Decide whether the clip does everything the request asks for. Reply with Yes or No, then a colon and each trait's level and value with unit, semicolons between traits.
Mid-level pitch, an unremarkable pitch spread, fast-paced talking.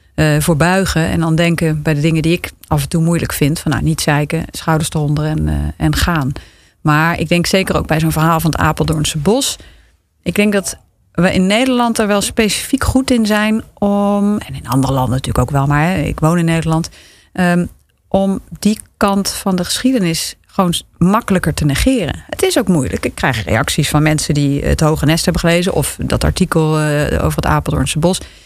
Yes: medium, 165 Hz; average, 4.0 semitones; fast, 205 wpm